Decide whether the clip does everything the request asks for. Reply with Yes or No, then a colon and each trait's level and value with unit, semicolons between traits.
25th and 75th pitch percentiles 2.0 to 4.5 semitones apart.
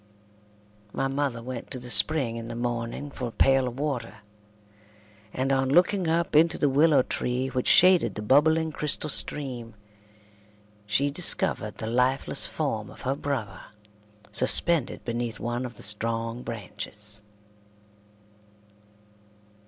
Yes: average, 3.8 semitones